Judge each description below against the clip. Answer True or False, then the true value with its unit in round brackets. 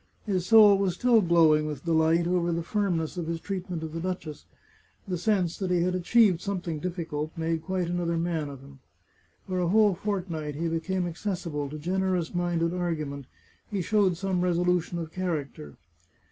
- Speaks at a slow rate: False (185 wpm)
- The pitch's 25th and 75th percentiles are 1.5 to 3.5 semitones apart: True (2.4 semitones)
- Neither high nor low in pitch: True (175 Hz)